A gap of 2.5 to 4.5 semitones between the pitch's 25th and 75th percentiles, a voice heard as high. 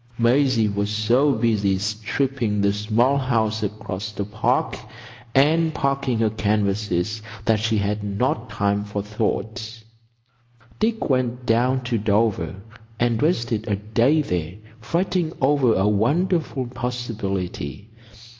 No: average, 3.7 semitones; low, 110 Hz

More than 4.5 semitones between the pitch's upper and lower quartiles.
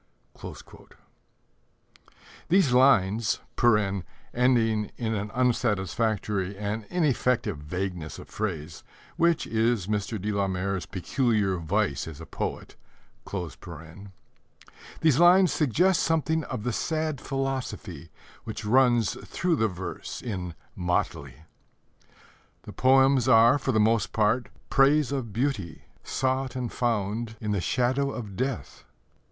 Yes: average, 5.0 semitones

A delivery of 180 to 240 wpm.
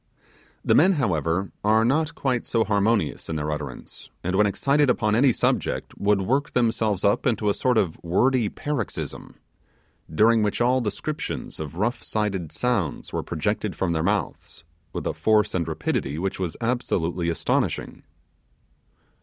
No: average, 155 wpm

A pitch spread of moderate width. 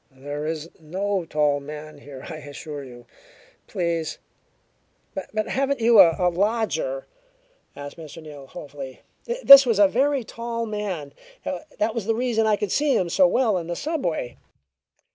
No: wide, 7.5 semitones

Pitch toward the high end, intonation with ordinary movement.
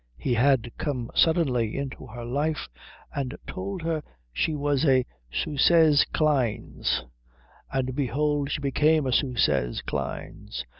No: medium, 140 Hz; average, 3.5 semitones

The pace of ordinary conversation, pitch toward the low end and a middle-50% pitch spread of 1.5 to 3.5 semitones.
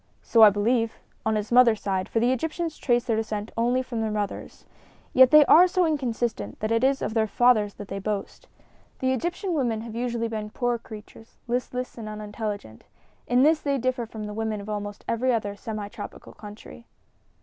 No: average, 190 wpm; high, 230 Hz; average, 3.0 semitones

